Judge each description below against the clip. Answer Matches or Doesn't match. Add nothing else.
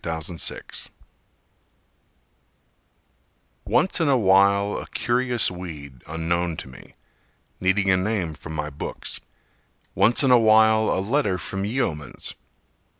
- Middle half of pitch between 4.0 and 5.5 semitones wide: Matches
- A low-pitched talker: Matches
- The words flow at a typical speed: Doesn't match